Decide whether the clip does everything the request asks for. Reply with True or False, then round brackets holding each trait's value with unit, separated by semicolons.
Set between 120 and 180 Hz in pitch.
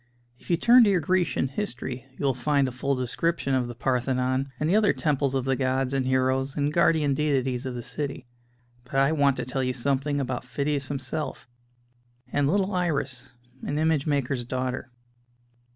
True (135 Hz)